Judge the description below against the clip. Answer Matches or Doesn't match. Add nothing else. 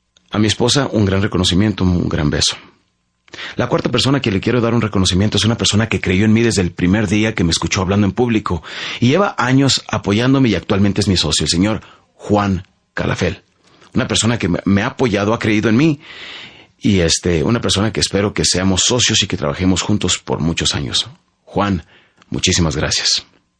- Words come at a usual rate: Doesn't match